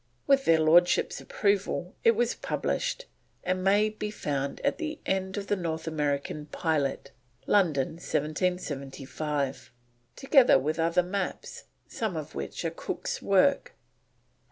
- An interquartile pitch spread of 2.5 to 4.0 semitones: No, wide, 5.5 semitones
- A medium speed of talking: No, slow, 130 wpm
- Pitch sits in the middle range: Yes, medium, 175 Hz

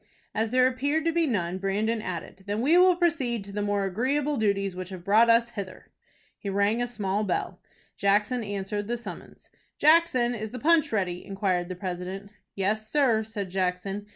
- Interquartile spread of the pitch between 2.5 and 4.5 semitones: Yes, average, 4.0 semitones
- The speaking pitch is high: Yes, high, 210 Hz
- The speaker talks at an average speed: Yes, average, 180 wpm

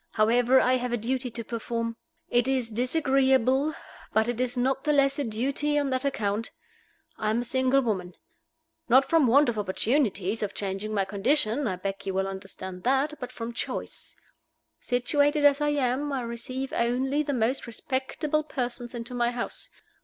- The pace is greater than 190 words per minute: No, average, 175 wpm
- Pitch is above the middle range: Yes, high, 245 Hz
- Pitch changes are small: No, average, 3.3 semitones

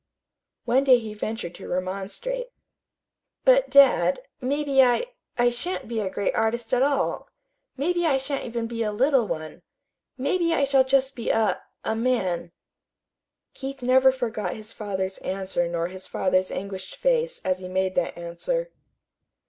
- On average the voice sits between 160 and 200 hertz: No, high, 240 Hz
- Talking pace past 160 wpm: No, average, 155 wpm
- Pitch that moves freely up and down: Yes, wide, 6.4 semitones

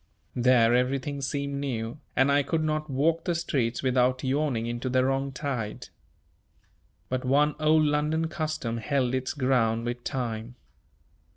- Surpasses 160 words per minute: No, average, 145 wpm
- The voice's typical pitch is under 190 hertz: Yes, low, 135 Hz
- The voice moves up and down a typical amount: Yes, average, 3.1 semitones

